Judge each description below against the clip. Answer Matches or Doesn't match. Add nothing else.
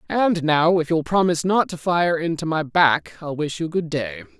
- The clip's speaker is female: Doesn't match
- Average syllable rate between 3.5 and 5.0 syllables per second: Matches